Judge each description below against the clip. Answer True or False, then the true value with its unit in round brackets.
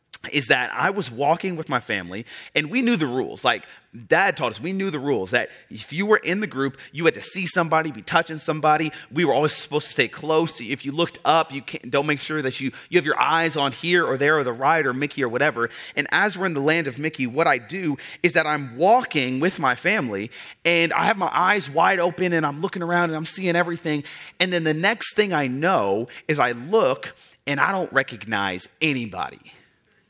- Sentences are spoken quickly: True (245 wpm)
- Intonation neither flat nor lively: True (3.8 semitones)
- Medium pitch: True (160 Hz)